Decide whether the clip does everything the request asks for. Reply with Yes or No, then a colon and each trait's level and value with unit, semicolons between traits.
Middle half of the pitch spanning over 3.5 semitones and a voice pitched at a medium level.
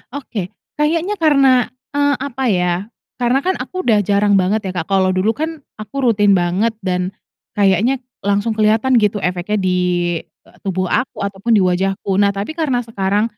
No: average, 5.2 semitones; high, 210 Hz